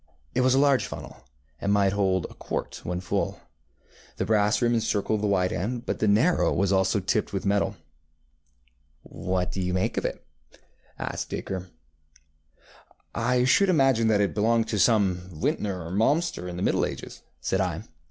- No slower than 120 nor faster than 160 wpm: No, average, 170 wpm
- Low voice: Yes, low, 100 Hz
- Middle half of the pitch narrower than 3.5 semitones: No, average, 3.9 semitones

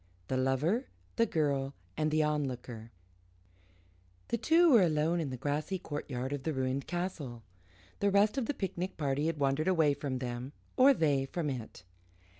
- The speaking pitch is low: No, medium, 150 Hz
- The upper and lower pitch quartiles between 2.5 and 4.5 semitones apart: No, average, 4.9 semitones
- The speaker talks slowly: No, average, 165 wpm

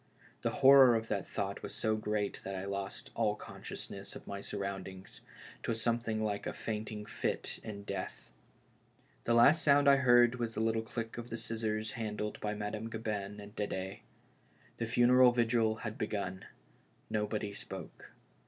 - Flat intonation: Yes, narrow, 2.3 semitones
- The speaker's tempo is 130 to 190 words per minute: Yes, average, 170 wpm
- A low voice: Yes, low, 110 Hz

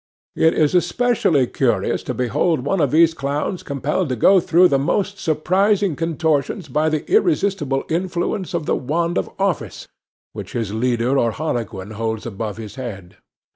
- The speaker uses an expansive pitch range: Yes, wide, 6.2 semitones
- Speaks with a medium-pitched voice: Yes, medium, 150 Hz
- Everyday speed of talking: Yes, average, 160 wpm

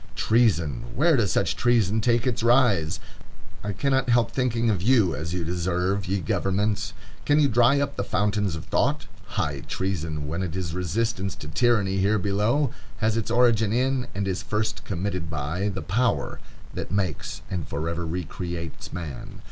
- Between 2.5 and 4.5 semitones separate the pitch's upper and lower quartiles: No, average, 4.9 semitones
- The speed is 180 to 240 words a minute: No, average, 165 wpm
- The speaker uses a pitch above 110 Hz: No, low, 100 Hz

